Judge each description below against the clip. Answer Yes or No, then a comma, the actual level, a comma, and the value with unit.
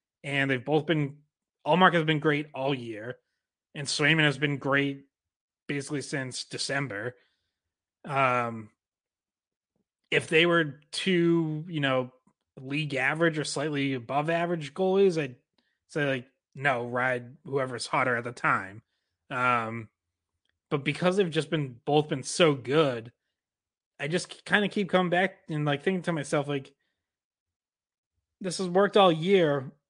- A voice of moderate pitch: Yes, medium, 145 Hz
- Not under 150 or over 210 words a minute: No, average, 140 wpm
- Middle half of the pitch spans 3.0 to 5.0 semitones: Yes, average, 4.5 semitones